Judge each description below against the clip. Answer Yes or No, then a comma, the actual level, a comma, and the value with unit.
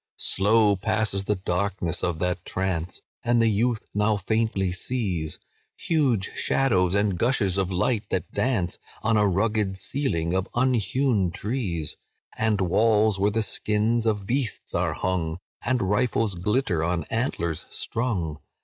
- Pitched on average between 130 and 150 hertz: No, low, 105 Hz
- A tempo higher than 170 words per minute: No, average, 140 wpm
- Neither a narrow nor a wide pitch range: Yes, average, 3.8 semitones